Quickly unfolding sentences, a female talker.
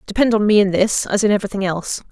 Yes: fast, 255 wpm; female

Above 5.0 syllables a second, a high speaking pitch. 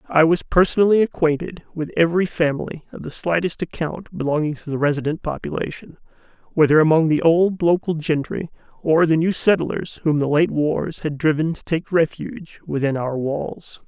No: 5.2 syllables/s; medium, 160 Hz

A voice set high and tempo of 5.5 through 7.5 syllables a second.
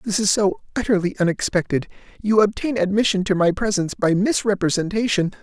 Yes: high, 195 Hz; 5.8 syllables/s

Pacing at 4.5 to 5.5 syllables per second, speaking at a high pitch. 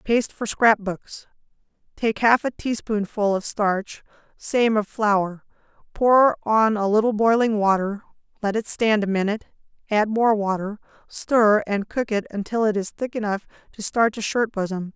Yes: 4.6 syllables/s; high, 215 Hz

